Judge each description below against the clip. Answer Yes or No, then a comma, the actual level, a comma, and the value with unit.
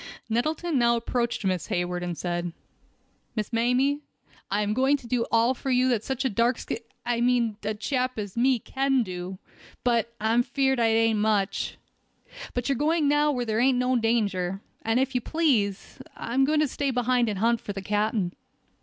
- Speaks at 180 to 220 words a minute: Yes, average, 190 wpm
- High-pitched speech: Yes, high, 235 Hz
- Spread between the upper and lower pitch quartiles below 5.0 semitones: Yes, average, 3.7 semitones